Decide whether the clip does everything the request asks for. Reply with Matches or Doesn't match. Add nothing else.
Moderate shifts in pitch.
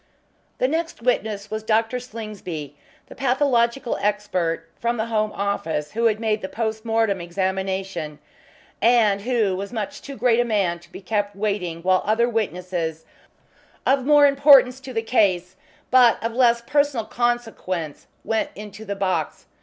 Matches